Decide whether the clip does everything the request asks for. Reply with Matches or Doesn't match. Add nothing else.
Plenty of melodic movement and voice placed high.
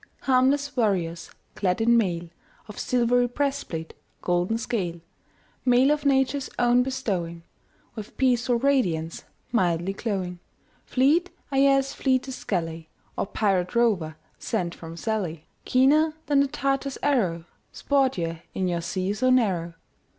Matches